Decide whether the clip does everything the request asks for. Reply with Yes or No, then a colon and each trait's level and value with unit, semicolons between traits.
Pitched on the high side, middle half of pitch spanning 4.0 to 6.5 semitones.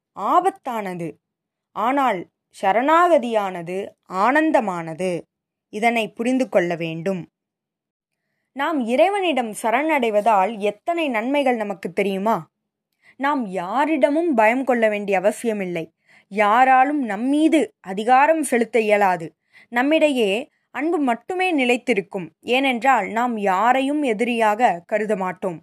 Yes: high, 230 Hz; wide, 5.4 semitones